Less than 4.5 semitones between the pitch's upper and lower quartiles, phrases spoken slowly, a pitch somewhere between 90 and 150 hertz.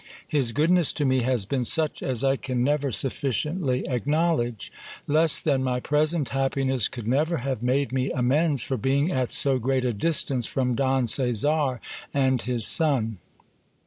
No: average, 2.8 semitones; average, 165 wpm; low, 135 Hz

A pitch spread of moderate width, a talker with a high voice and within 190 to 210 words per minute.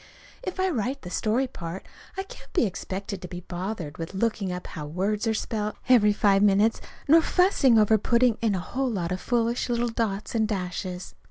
Yes: average, 4.3 semitones; high, 210 Hz; average, 195 wpm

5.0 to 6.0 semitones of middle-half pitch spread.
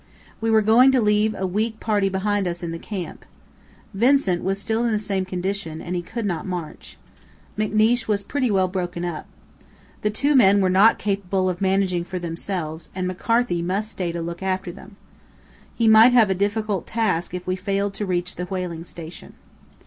No: average, 3.2 semitones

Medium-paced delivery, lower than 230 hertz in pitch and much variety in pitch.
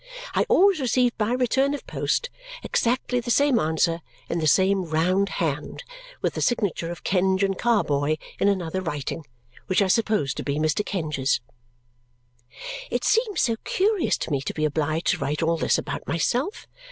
Yes: average, 170 wpm; high, 190 Hz; wide, 7.4 semitones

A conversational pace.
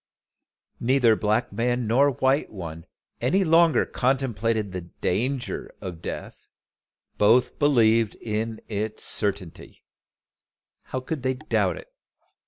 No: slow, 110 wpm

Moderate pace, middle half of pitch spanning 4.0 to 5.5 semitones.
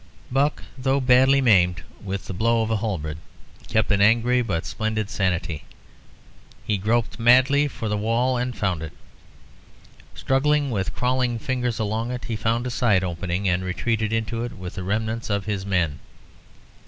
Yes: average, 165 wpm; average, 4.3 semitones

